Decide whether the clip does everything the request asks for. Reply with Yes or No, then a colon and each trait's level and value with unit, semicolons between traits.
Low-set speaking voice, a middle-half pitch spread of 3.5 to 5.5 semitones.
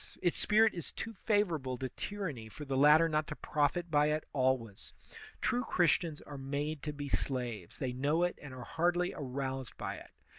No: medium, 150 Hz; average, 4.5 semitones